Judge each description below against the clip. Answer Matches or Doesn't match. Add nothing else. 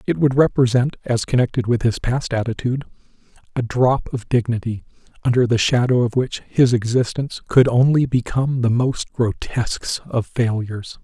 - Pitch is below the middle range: Matches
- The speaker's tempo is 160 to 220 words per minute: Doesn't match